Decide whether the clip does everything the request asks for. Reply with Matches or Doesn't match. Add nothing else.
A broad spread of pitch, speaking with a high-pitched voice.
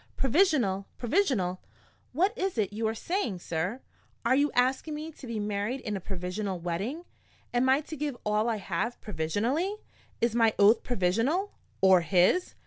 Matches